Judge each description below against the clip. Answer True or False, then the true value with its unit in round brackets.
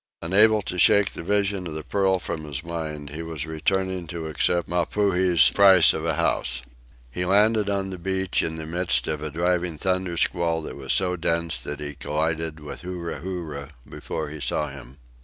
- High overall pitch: False (85 Hz)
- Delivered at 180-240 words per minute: True (190 wpm)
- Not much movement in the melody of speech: False (3.3 semitones)